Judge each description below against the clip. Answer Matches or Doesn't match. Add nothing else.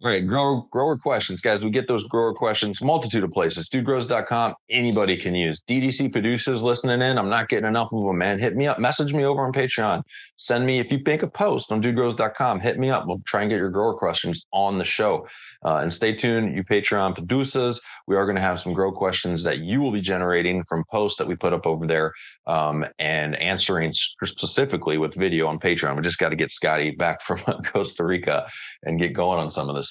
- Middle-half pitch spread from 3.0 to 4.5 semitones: Doesn't match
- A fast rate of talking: Matches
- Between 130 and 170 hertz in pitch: Doesn't match